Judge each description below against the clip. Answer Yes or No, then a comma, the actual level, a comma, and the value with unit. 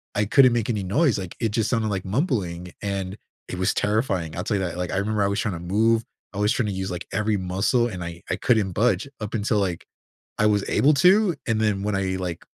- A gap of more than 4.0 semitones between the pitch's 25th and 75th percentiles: No, average, 3.2 semitones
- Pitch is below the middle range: Yes, low, 100 Hz